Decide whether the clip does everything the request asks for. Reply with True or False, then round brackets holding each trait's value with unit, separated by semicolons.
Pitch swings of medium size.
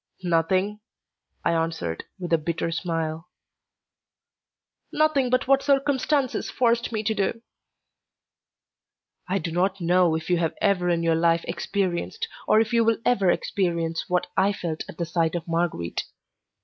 True (4.8 semitones)